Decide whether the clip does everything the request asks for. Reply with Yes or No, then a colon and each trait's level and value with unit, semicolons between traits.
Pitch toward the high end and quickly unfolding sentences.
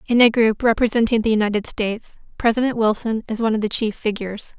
No: high, 220 Hz; average, 195 wpm